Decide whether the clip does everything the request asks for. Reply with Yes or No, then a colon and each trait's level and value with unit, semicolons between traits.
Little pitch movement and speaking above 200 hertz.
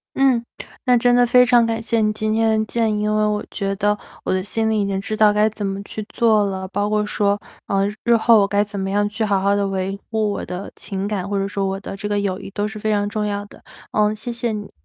Yes: narrow, 1.6 semitones; high, 210 Hz